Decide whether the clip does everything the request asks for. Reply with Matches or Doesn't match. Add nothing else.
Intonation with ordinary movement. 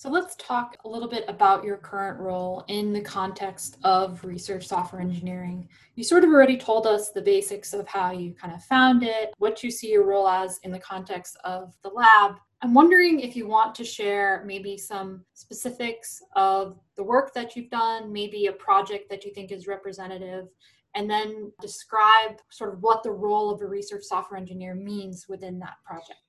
Matches